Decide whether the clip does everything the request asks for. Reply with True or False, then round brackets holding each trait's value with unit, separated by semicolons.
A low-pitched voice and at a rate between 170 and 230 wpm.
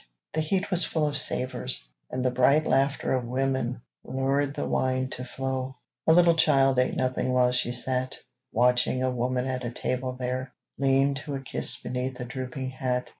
True (130 Hz; 180 wpm)